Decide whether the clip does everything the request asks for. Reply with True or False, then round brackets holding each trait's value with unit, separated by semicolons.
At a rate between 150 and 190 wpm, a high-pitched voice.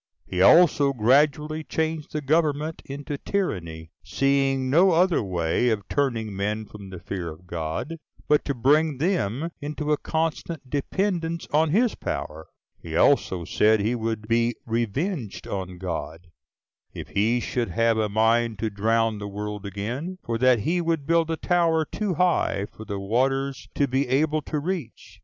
False (160 wpm; 130 Hz)